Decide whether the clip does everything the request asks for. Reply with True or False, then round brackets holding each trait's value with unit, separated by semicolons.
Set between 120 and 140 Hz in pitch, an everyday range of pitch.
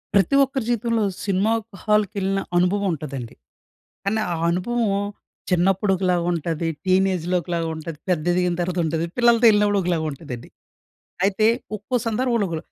False (190 Hz; 3.8 semitones)